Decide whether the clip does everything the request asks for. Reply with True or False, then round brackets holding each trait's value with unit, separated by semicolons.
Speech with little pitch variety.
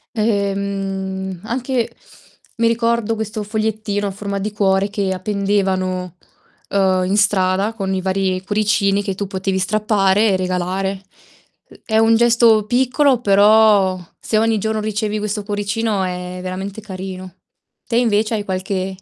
True (2.3 semitones)